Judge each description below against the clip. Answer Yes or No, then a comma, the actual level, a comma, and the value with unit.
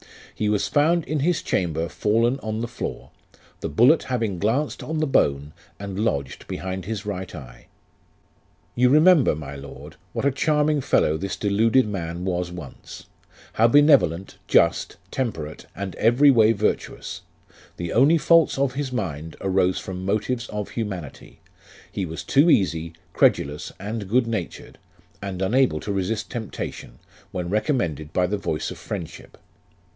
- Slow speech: No, average, 155 wpm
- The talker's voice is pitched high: No, low, 105 Hz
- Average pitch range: No, wide, 6.3 semitones